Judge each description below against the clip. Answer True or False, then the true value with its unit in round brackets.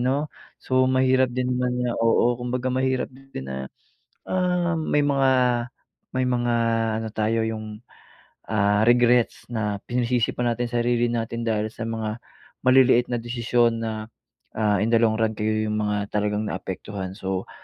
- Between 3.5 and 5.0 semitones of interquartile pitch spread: False (2.7 semitones)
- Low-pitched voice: True (120 Hz)